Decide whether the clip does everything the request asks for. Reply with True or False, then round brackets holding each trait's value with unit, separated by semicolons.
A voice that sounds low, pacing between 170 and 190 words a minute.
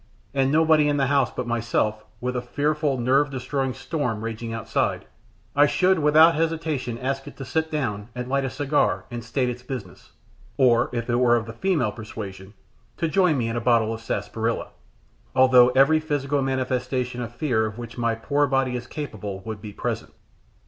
True (125 Hz; 185 wpm)